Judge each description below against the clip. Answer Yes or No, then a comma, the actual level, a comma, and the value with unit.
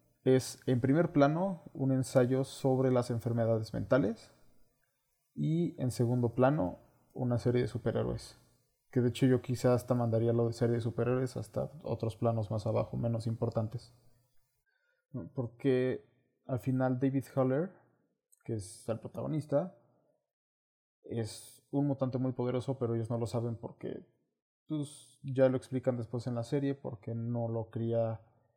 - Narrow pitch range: Yes, narrow, 2.3 semitones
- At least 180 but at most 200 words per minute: No, average, 145 wpm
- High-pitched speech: No, low, 125 Hz